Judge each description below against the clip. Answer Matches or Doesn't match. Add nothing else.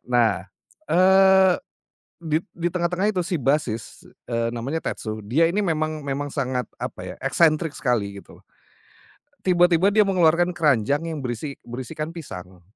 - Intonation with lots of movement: Matches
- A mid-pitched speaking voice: Matches